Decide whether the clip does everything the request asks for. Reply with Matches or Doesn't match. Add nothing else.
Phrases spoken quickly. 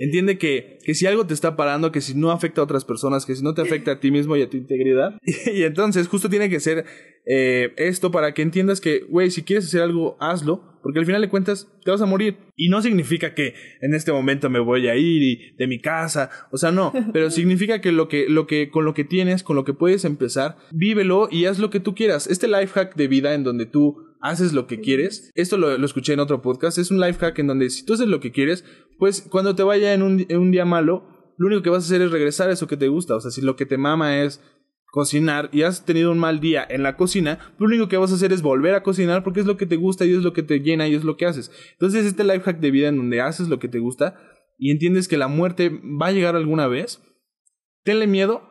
Matches